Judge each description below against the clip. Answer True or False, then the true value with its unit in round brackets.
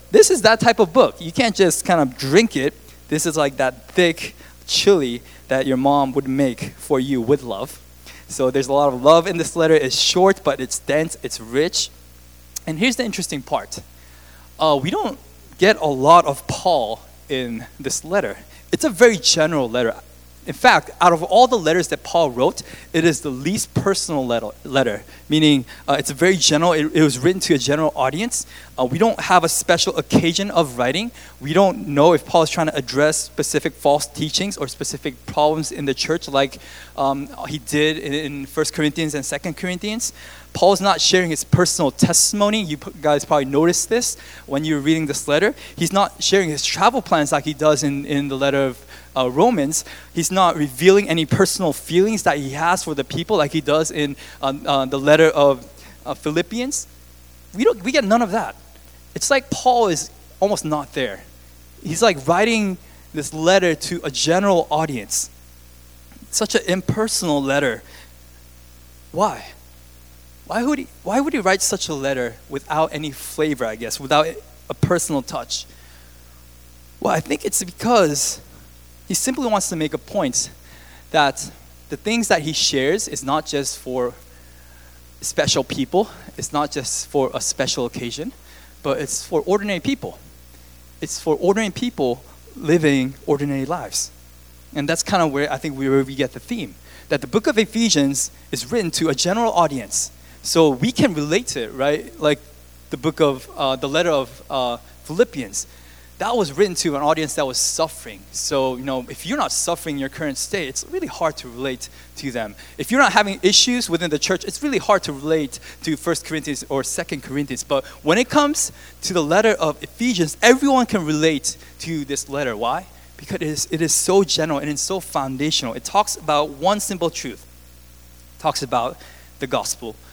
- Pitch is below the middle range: False (150 Hz)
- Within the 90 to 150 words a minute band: False (185 wpm)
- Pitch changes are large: True (5.9 semitones)